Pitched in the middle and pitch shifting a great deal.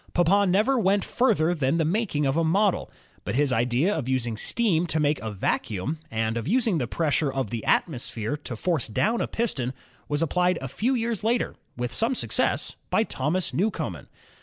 Yes: medium, 160 Hz; wide, 7.7 semitones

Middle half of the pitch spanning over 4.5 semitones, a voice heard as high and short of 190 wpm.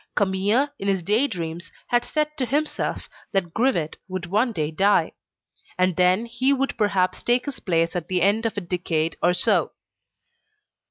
Yes: average, 5.3 semitones; high, 195 Hz; average, 170 wpm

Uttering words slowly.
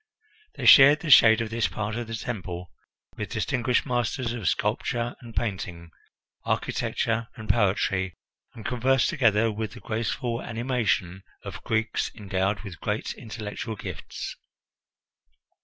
Yes: slow, 130 wpm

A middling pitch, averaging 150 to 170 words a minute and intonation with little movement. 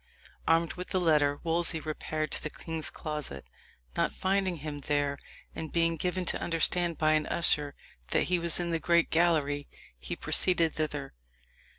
Yes: medium, 160 Hz; average, 165 wpm; narrow, 2.3 semitones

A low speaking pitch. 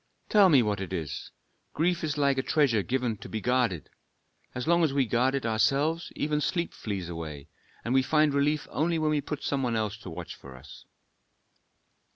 Yes: low, 130 Hz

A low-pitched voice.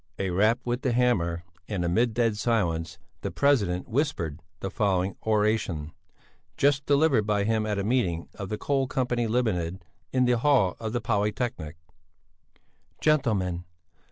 Yes: low, 110 Hz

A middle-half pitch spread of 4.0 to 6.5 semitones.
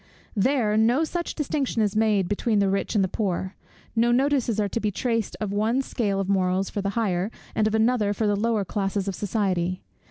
No: average, 2.8 semitones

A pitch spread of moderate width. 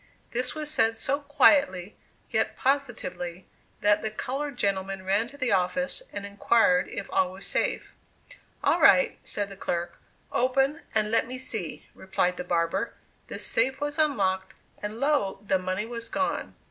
No: wide, 6.1 semitones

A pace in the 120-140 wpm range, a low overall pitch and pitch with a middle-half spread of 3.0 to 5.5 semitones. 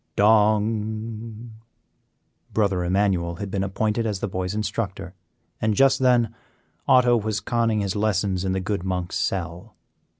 No: slow, 135 wpm; low, 105 Hz; narrow, 2.6 semitones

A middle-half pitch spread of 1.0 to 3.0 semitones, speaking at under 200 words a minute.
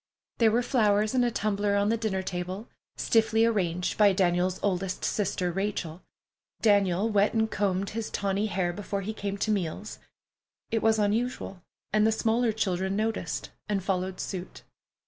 Yes: narrow, 2.6 semitones; average, 160 wpm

